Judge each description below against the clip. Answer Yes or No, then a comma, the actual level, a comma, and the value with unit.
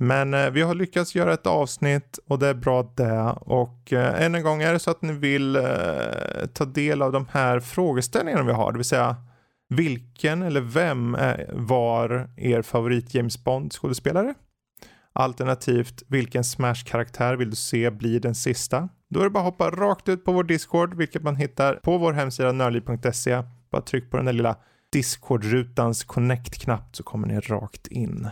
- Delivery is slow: No, average, 175 wpm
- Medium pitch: No, low, 130 Hz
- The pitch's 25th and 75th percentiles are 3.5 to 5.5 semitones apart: Yes, average, 4.0 semitones